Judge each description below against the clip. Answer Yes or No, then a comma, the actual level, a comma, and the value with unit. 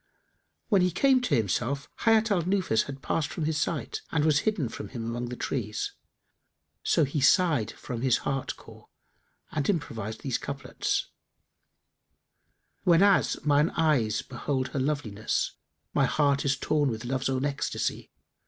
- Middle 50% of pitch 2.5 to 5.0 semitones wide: Yes, average, 4.6 semitones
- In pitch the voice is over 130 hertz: Yes, medium, 140 Hz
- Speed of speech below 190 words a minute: Yes, average, 155 wpm